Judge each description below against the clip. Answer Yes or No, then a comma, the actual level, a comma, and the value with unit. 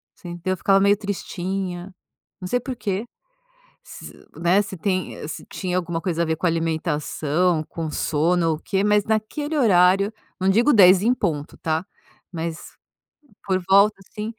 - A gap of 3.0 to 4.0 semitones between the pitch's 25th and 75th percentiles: Yes, average, 3.3 semitones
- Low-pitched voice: No, medium, 185 Hz